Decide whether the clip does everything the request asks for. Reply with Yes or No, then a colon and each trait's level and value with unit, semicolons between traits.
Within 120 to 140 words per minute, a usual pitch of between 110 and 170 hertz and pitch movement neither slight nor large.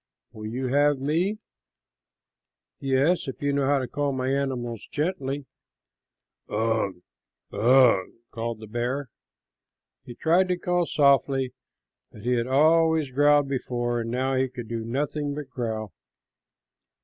Yes: slow, 135 wpm; low, 135 Hz; average, 3.3 semitones